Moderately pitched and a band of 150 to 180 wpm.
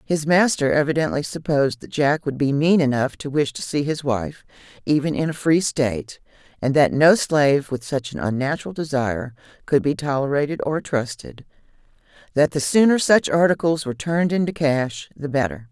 Yes: medium, 150 Hz; average, 175 wpm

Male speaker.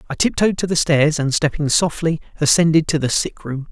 Yes: male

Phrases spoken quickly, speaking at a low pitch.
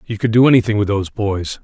Yes: fast, 255 wpm; low, 105 Hz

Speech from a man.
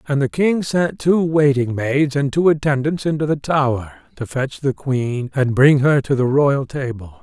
Yes: male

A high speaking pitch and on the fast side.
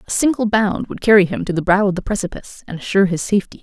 Yes: high, 195 Hz; fast, 265 wpm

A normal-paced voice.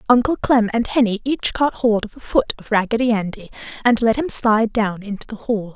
No: fast, 220 wpm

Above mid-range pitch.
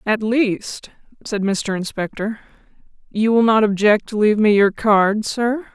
Yes: high, 215 Hz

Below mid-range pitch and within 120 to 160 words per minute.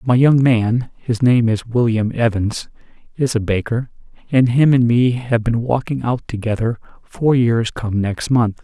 No: low, 120 Hz; average, 175 wpm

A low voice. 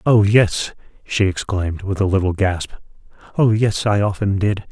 Yes: low, 100 Hz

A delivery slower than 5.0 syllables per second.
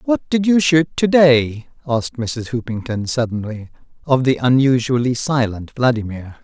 Yes: 4.6 syllables/s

